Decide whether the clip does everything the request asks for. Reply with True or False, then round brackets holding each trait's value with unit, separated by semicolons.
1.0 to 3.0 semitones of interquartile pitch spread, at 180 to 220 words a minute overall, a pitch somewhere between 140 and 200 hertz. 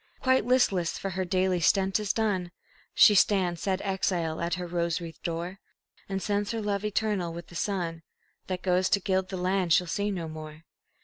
True (2.6 semitones; 190 wpm; 185 Hz)